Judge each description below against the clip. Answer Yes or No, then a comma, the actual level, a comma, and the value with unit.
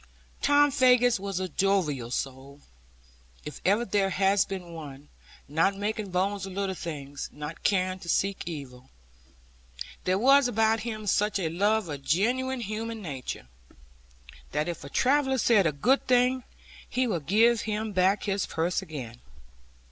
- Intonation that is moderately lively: No, wide, 5.7 semitones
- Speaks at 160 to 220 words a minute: No, average, 150 wpm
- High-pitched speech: Yes, high, 195 Hz